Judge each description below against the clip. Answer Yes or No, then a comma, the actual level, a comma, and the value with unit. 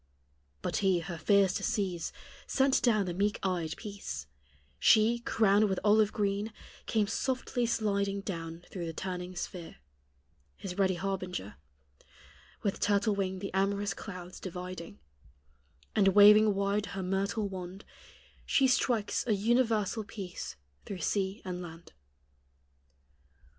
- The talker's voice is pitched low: No, high, 195 Hz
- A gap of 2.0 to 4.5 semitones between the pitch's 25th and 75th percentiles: Yes, narrow, 2.4 semitones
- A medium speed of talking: No, slow, 125 wpm